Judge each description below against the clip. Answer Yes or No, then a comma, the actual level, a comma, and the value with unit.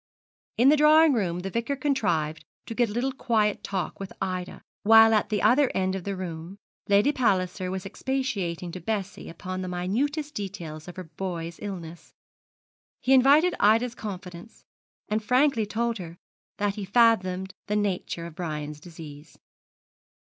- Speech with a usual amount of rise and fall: Yes, average, 4.8 semitones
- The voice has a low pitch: No, high, 200 Hz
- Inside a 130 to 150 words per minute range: No, average, 160 wpm